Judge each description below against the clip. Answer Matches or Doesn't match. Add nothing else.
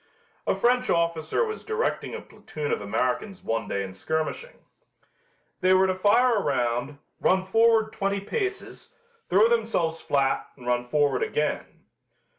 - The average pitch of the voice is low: Doesn't match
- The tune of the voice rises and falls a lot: Matches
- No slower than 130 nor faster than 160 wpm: Matches